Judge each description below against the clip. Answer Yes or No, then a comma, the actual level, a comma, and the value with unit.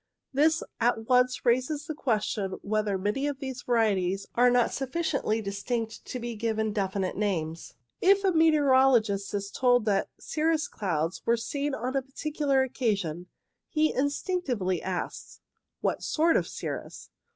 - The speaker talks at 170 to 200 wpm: No, average, 150 wpm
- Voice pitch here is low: No, high, 240 Hz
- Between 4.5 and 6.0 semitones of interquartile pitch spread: Yes, wide, 5.6 semitones